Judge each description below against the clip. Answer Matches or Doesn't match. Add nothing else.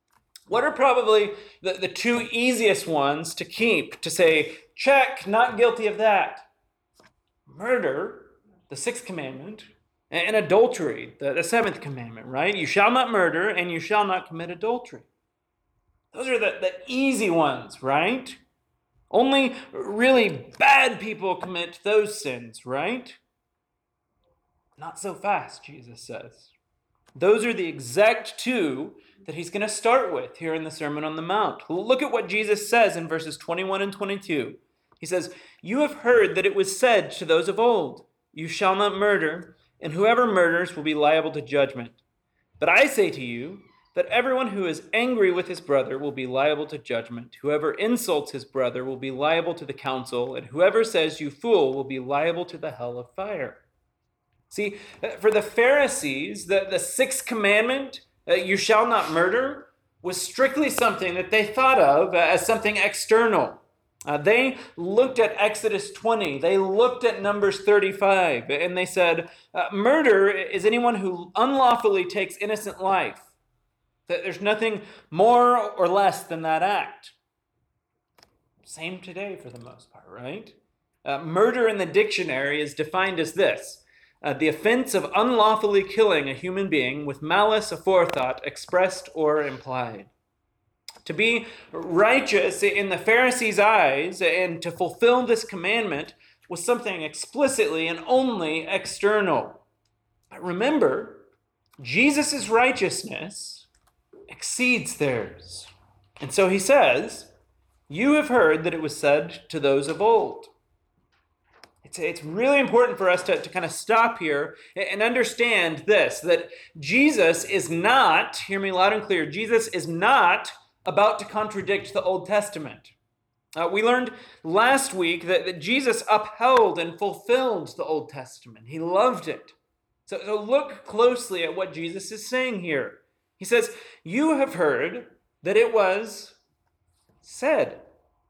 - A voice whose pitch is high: Matches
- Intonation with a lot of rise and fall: Matches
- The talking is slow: Doesn't match